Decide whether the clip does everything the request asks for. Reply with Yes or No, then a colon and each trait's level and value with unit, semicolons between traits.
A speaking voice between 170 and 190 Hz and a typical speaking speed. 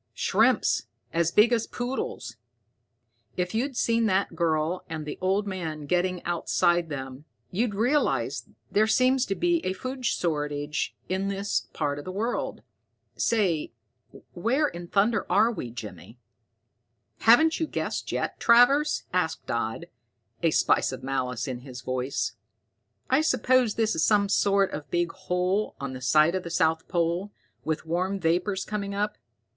Yes: medium, 185 Hz; average, 150 wpm